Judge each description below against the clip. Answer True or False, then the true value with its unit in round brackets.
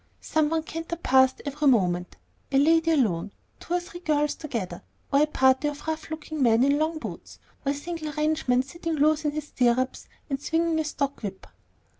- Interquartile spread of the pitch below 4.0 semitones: True (3.3 semitones)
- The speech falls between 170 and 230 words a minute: True (190 wpm)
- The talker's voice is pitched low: False (295 Hz)